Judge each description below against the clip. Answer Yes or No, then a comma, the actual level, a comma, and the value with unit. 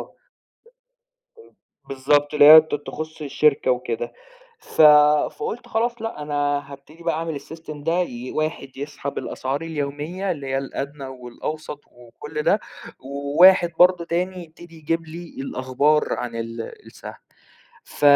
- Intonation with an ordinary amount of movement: Yes, average, 3.2 semitones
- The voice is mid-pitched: Yes, medium, 150 Hz